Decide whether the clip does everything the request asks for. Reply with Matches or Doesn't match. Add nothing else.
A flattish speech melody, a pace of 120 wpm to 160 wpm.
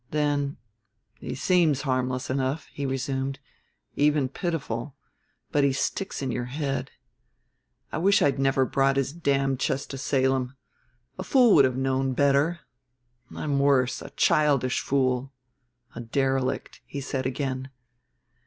Matches